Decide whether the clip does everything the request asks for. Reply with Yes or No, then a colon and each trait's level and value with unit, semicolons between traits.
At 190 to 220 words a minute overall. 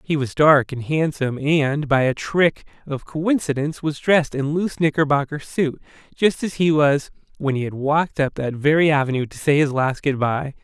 Yes: average, 195 wpm